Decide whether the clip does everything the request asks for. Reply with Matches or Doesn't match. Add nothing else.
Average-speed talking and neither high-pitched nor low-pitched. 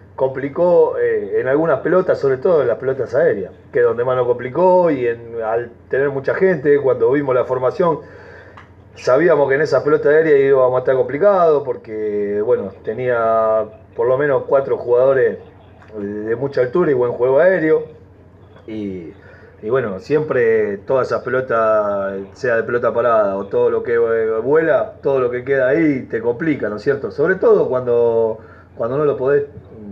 Matches